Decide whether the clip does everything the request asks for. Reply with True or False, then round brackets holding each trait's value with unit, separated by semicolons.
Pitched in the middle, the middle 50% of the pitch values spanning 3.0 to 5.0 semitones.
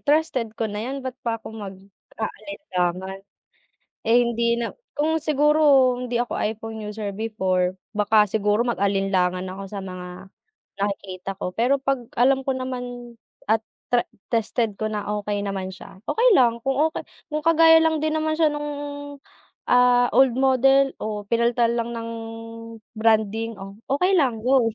False (230 Hz; 4.4 semitones)